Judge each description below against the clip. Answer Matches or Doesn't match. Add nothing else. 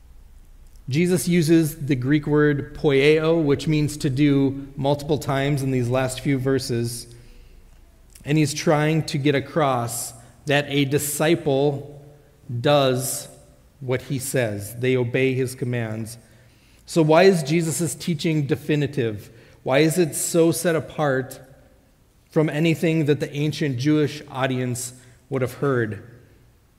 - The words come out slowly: Matches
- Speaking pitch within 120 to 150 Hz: Matches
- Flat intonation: Doesn't match